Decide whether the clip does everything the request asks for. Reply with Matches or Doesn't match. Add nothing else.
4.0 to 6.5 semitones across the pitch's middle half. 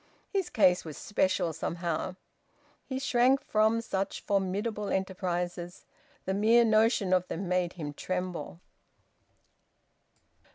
Doesn't match